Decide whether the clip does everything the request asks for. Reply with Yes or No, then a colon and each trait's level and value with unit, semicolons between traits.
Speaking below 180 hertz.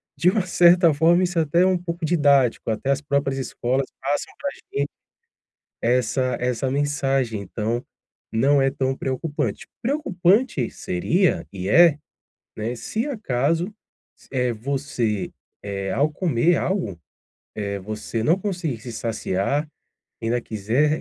Yes: medium, 140 Hz